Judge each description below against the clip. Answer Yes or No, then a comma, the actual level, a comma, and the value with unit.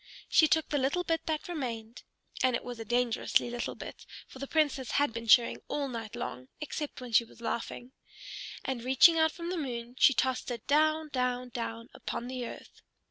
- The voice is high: Yes, very high, 255 Hz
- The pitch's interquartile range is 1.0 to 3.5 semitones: No, average, 4.2 semitones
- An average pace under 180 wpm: No, average, 195 wpm